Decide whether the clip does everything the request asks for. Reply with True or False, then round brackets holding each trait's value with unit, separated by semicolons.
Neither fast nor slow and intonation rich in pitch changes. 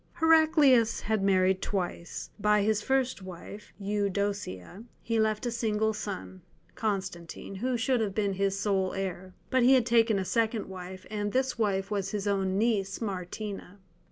False (155 wpm; 2.8 semitones)